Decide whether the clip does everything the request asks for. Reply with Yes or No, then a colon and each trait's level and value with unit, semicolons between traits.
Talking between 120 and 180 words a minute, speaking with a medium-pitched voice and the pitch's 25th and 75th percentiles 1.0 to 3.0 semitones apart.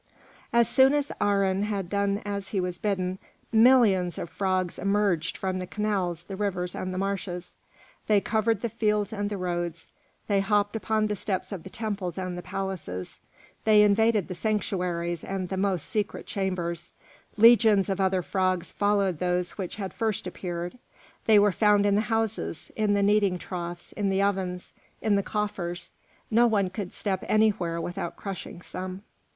No: average, 170 wpm; high, 195 Hz; narrow, 2.5 semitones